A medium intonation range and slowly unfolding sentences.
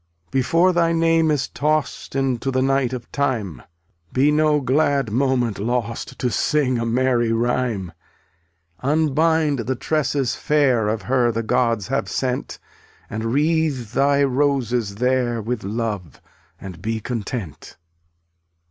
Yes: average, 3.8 semitones; slow, 130 wpm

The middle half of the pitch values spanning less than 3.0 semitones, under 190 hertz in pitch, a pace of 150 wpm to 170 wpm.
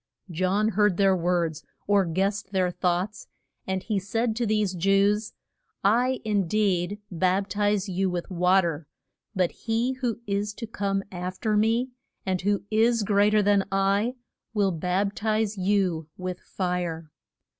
No: narrow, 2.6 semitones; high, 195 Hz; average, 155 wpm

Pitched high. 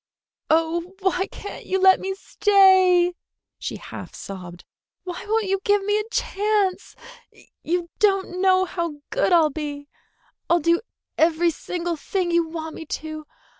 Yes: very high, 355 Hz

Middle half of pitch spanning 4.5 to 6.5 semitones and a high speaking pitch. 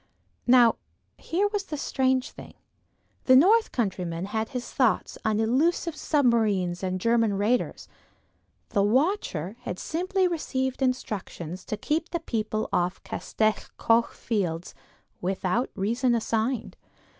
Yes: average, 4.8 semitones; high, 230 Hz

